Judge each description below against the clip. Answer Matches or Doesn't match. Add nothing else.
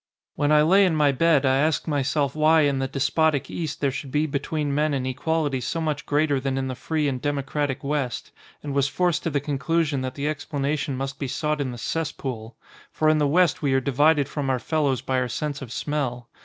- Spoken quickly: Matches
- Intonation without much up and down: Matches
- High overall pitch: Doesn't match